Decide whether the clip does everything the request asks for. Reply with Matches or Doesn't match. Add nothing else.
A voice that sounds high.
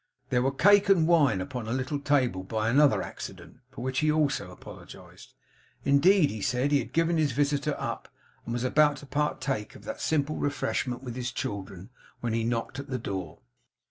Doesn't match